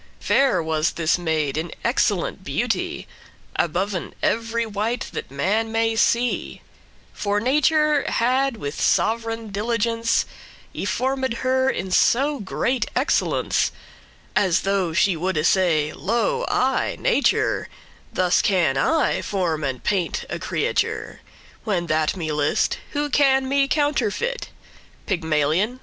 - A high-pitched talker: Yes, high, 210 Hz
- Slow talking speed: Yes, slow, 120 wpm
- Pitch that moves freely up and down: Yes, wide, 6.9 semitones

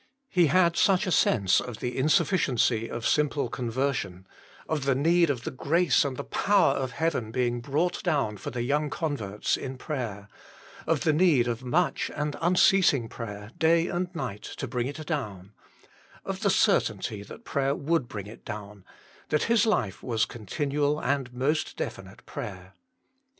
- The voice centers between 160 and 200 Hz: No, low, 135 Hz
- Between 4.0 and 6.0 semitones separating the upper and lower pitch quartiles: Yes, wide, 5.6 semitones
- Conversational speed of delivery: Yes, average, 165 wpm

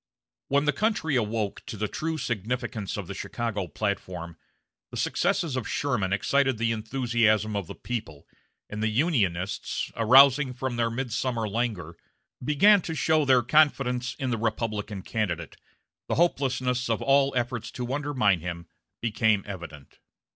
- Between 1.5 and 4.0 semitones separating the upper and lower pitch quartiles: No, average, 4.4 semitones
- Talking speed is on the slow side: No, average, 145 wpm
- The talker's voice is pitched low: Yes, low, 115 Hz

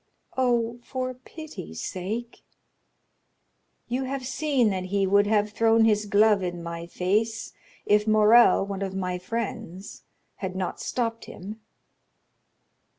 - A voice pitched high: Yes, high, 210 Hz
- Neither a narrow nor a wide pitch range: Yes, average, 3.6 semitones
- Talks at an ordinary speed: No, slow, 125 wpm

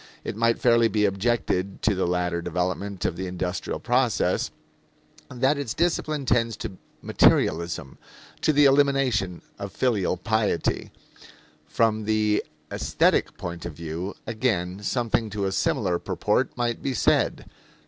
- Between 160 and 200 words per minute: No, slow, 135 wpm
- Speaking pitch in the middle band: No, low, 105 Hz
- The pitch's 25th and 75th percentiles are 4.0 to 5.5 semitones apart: Yes, average, 4.8 semitones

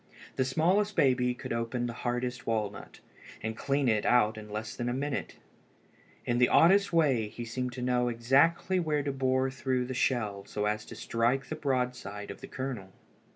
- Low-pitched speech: Yes, low, 125 Hz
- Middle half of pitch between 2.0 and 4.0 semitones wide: Yes, average, 2.8 semitones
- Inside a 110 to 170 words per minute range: No, average, 190 wpm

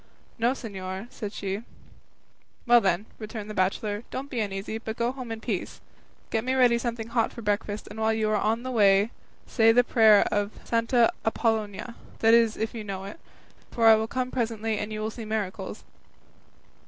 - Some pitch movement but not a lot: No, narrow, 2.0 semitones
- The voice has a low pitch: No, high, 220 Hz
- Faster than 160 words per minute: Yes, average, 190 wpm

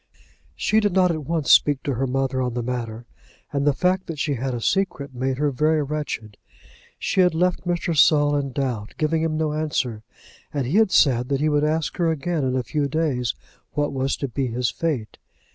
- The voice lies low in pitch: No, medium, 145 Hz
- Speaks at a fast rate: Yes, fast, 210 wpm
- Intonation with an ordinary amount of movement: Yes, average, 3.7 semitones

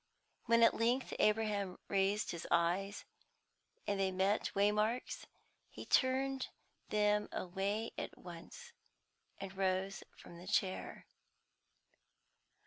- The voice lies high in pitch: Yes, high, 200 Hz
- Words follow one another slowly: Yes, slow, 105 wpm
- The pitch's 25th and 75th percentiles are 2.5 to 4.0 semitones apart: Yes, average, 2.8 semitones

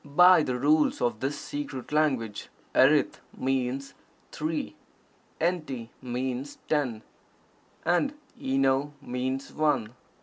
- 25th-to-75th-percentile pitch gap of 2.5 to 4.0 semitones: Yes, average, 3.3 semitones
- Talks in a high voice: No, low, 135 Hz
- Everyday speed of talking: No, slow, 100 wpm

